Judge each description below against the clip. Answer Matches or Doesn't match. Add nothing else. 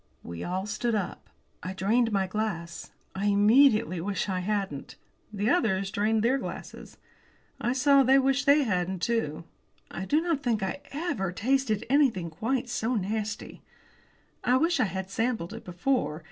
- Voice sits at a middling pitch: Doesn't match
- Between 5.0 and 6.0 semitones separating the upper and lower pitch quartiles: Matches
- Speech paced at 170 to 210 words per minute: Doesn't match